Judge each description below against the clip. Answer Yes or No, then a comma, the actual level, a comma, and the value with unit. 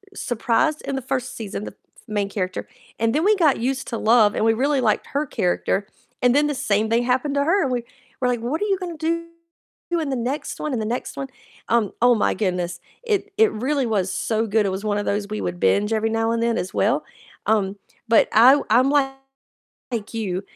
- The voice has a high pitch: Yes, high, 235 Hz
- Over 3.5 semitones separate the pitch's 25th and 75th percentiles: Yes, average, 4.7 semitones